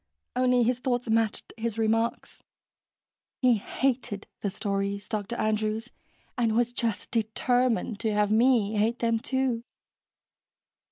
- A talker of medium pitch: No, high, 230 Hz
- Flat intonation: Yes, narrow, 2.3 semitones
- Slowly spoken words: Yes, slow, 120 wpm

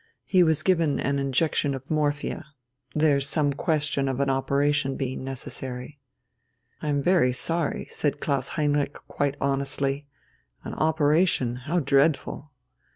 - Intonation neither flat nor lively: No, narrow, 2.1 semitones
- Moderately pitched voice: Yes, medium, 145 Hz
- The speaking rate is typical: No, slow, 130 wpm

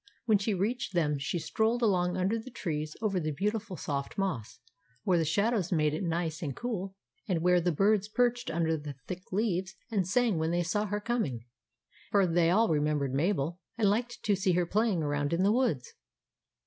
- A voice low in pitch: No, medium, 185 Hz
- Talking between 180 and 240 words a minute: Yes, average, 195 wpm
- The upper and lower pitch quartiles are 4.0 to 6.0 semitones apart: Yes, average, 4.6 semitones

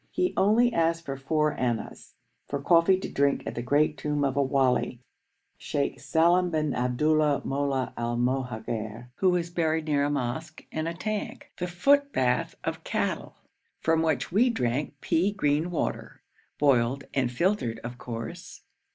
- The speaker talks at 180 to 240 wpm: No, average, 155 wpm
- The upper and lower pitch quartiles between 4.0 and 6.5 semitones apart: Yes, average, 4.8 semitones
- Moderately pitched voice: Yes, medium, 145 Hz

